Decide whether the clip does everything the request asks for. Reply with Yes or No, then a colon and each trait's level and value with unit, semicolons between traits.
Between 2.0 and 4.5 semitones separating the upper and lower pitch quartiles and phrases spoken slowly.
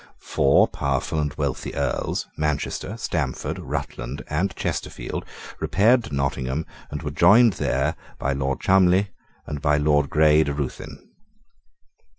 Yes: average, 3.8 semitones; slow, 130 wpm